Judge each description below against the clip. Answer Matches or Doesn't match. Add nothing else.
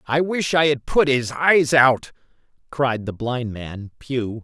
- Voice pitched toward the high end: Doesn't match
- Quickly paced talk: Doesn't match